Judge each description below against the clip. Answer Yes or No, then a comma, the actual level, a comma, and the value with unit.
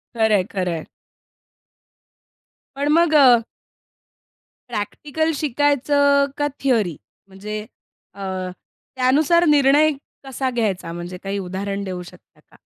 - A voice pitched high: Yes, very high, 250 Hz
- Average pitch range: No, wide, 6.5 semitones